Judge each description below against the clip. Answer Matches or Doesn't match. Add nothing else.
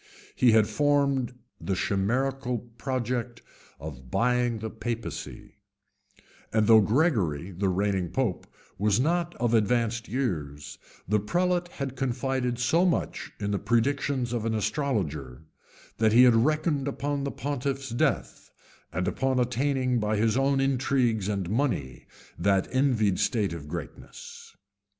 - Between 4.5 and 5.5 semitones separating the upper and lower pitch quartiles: Matches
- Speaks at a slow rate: Matches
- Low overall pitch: Matches